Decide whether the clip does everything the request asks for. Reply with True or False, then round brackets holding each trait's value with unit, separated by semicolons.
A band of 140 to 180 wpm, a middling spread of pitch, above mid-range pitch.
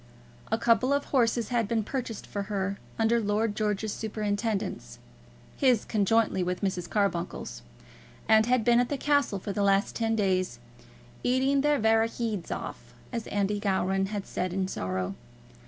True (155 wpm; 3.0 semitones; 215 Hz)